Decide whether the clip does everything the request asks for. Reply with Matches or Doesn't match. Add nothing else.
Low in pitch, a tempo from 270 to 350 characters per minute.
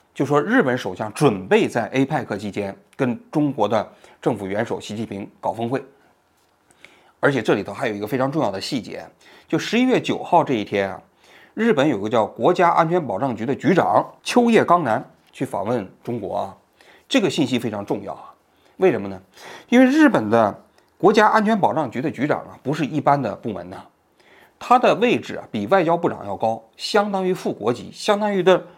Doesn't match